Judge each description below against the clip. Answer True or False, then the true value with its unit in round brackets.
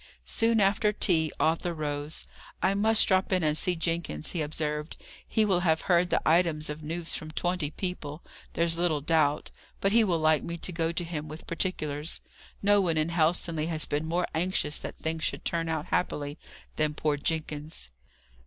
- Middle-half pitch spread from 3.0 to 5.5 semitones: False (2.6 semitones)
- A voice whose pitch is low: False (165 Hz)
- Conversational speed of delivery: True (180 wpm)